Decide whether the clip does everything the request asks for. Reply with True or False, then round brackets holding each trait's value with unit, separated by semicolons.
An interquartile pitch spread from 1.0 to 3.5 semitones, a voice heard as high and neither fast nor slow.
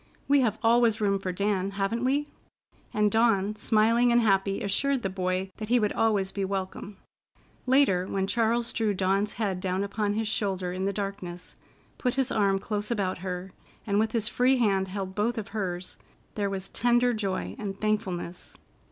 True (2.8 semitones; 205 Hz; 180 wpm)